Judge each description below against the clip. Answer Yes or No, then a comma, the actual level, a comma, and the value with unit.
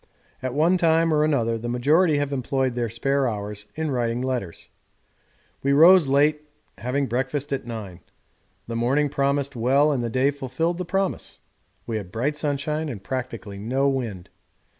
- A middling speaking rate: Yes, average, 160 wpm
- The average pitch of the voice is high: No, low, 135 Hz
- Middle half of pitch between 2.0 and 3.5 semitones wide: No, average, 3.9 semitones